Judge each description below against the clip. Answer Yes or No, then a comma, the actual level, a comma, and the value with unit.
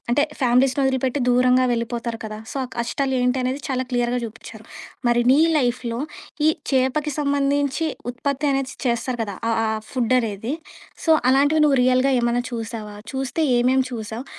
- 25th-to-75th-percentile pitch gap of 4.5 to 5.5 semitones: No, narrow, 2.4 semitones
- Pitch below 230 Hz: No, very high, 255 Hz